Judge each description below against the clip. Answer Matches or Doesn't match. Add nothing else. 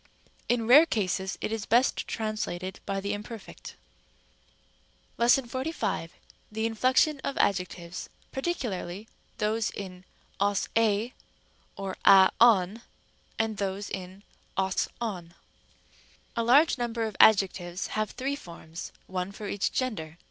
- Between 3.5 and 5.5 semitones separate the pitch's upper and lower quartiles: Matches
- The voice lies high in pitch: Matches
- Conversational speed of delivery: Doesn't match